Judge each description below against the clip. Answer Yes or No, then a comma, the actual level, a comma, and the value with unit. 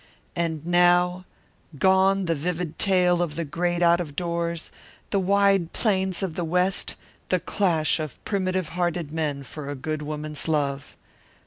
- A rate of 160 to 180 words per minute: No, average, 150 wpm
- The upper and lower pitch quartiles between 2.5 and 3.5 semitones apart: Yes, average, 2.9 semitones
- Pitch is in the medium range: Yes, medium, 175 Hz